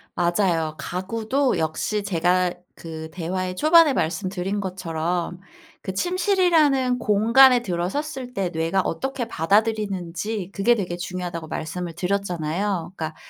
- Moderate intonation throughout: Yes, average, 4.9 semitones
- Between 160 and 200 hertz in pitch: Yes, high, 190 Hz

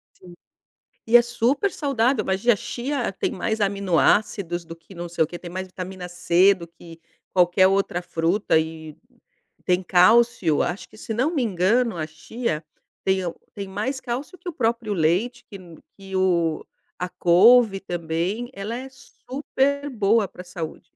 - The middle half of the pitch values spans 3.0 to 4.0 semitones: No, average, 5.3 semitones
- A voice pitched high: Yes, high, 195 Hz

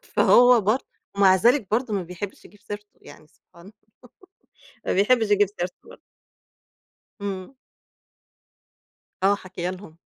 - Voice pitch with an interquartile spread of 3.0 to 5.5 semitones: No, narrow, 2.5 semitones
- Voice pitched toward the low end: No, high, 200 Hz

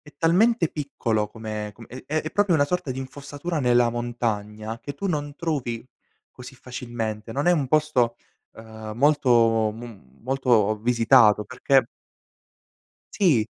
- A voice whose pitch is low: Yes, low, 125 Hz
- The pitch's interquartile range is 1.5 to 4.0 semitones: No, average, 4.5 semitones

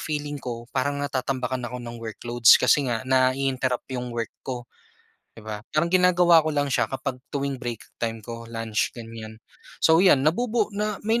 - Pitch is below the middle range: Yes, low, 130 Hz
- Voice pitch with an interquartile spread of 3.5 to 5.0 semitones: Yes, average, 3.9 semitones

